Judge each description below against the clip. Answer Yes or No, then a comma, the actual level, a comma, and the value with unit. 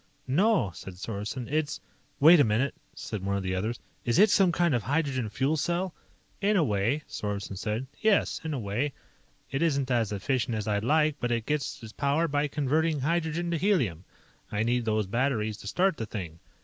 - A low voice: Yes, low, 130 Hz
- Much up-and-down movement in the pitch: Yes, wide, 6.7 semitones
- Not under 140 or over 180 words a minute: No, average, 200 wpm